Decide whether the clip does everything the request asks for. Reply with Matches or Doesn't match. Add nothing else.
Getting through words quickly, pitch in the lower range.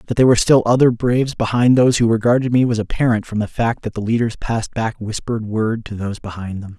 Matches